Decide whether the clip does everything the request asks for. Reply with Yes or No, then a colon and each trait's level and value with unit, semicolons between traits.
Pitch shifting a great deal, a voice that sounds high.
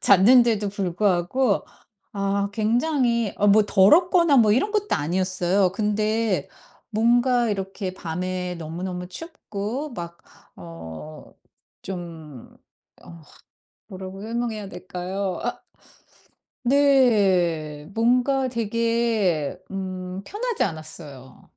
No: average, 4.7 semitones; high, 200 Hz